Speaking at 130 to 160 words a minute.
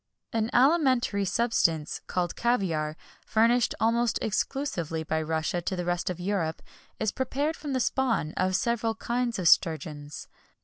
Yes: average, 140 wpm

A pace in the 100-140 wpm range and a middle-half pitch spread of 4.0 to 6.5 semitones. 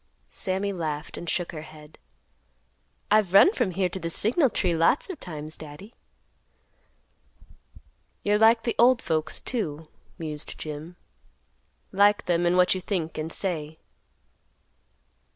Yes: slow, 135 wpm; average, 4.6 semitones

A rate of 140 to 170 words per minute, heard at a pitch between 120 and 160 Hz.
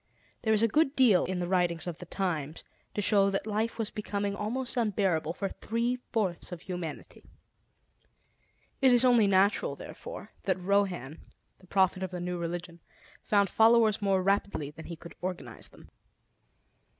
No: average, 160 wpm; high, 195 Hz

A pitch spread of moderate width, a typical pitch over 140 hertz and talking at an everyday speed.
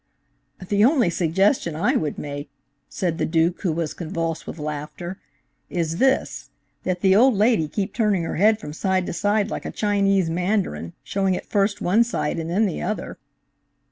Yes: average, 4.0 semitones; medium, 185 Hz; average, 175 wpm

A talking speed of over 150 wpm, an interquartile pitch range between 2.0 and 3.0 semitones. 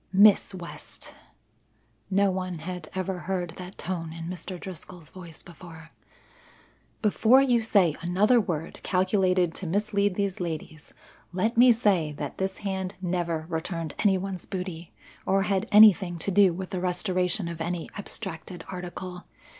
No: average, 145 wpm; narrow, 2.4 semitones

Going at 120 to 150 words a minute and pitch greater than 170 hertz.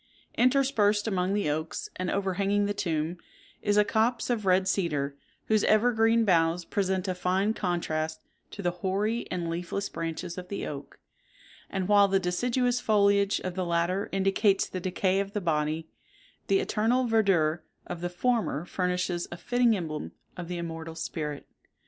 No: average, 160 wpm; high, 190 Hz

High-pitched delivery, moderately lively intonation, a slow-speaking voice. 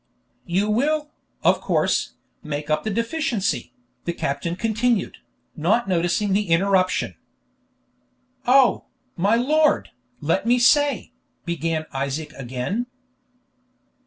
No: high, 195 Hz; wide, 6.4 semitones; slow, 105 wpm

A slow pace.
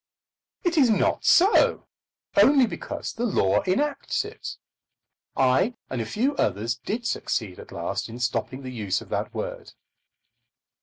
No: average, 145 wpm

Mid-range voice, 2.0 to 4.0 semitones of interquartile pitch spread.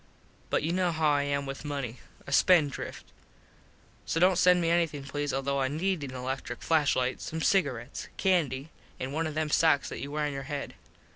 Yes: medium, 145 Hz; average, 3.1 semitones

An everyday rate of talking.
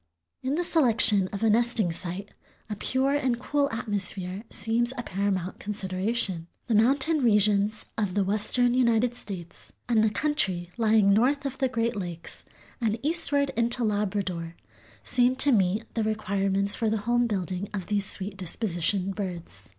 Yes: average, 155 wpm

